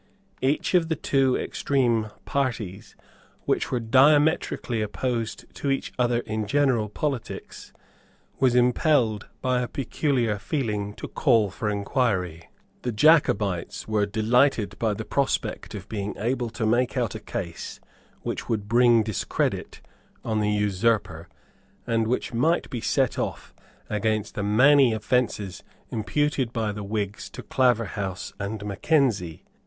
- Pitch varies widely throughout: No, average, 3.8 semitones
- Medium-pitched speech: No, low, 115 Hz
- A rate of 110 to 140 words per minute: Yes, slow, 135 wpm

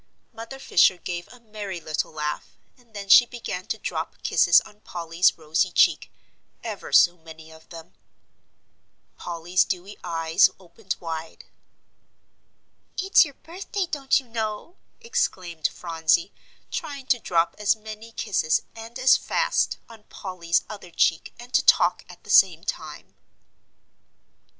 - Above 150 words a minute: No, slow, 135 wpm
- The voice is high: Yes, high, 195 Hz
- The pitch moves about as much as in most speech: No, wide, 6.0 semitones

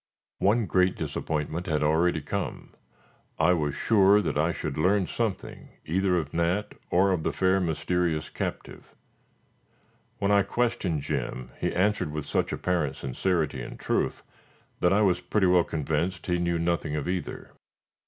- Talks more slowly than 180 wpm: Yes, average, 155 wpm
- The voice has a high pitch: No, very low, 90 Hz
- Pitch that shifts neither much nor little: Yes, average, 3.5 semitones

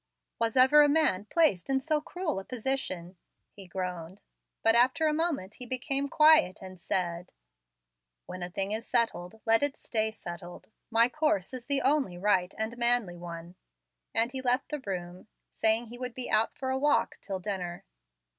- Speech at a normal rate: Yes, average, 175 wpm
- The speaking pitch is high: Yes, high, 225 Hz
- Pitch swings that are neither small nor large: No, wide, 6.4 semitones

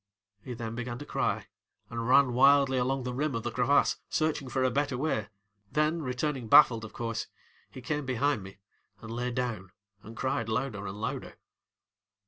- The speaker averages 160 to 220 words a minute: Yes, average, 180 wpm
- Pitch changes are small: No, average, 3.2 semitones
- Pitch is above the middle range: No, low, 125 Hz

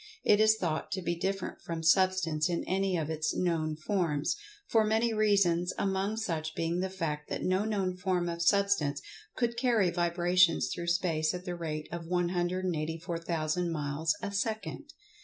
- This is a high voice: No, medium, 175 Hz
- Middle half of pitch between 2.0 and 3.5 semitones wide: Yes, average, 3.1 semitones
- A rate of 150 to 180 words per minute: Yes, average, 160 wpm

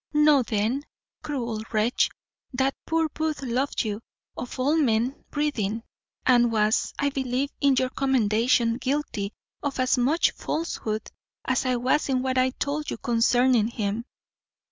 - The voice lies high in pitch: Yes, very high, 255 Hz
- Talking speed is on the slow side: No, average, 145 wpm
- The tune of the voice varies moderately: Yes, average, 3.5 semitones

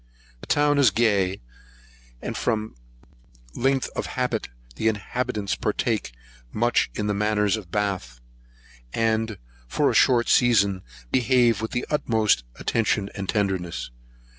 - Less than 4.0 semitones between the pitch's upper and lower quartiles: Yes, average, 3.1 semitones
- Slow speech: Yes, slow, 125 wpm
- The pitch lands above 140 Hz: No, low, 110 Hz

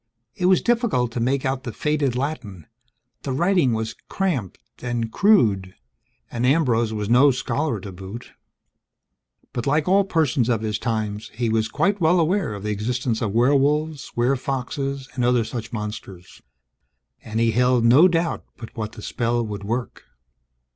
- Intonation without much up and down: No, average, 4.6 semitones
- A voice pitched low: Yes, low, 125 Hz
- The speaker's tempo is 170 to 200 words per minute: No, average, 160 wpm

